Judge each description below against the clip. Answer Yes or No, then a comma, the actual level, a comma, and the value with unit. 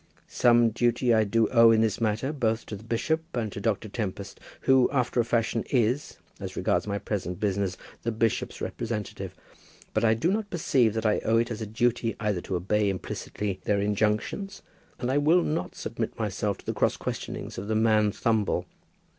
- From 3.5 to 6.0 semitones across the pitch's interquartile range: No, narrow, 2.4 semitones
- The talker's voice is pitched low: Yes, low, 110 Hz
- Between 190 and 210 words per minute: Yes, average, 195 wpm